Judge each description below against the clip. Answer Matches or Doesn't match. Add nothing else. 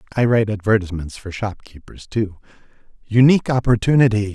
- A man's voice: Matches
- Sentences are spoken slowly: Matches